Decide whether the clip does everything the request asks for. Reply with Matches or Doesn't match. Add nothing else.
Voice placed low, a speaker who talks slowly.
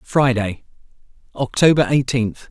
Matches